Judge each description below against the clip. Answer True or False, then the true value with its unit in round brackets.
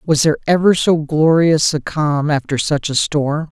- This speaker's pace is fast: False (185 wpm)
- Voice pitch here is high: False (155 Hz)